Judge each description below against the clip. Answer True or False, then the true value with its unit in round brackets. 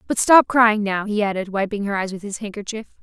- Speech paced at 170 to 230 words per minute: False (240 wpm)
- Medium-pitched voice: False (205 Hz)